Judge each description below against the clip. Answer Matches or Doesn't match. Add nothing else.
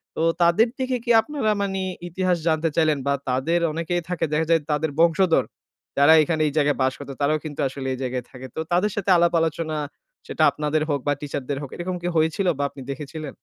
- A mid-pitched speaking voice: Matches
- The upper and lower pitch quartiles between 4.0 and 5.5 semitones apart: Doesn't match